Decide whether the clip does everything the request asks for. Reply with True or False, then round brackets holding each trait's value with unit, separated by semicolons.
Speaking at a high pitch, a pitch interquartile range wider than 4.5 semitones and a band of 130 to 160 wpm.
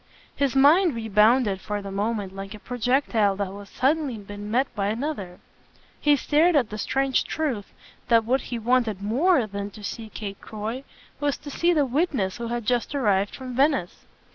False (230 Hz; 4.9 semitones; 180 wpm)